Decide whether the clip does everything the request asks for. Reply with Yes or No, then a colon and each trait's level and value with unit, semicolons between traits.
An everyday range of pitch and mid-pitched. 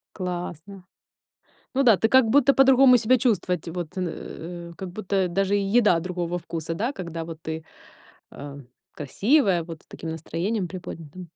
Yes: average, 4.5 semitones; medium, 180 Hz